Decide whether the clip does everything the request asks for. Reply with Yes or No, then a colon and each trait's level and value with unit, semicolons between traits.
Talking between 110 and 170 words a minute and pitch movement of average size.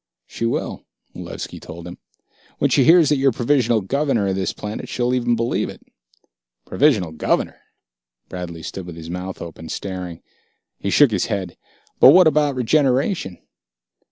No: average, 155 wpm; wide, 7.0 semitones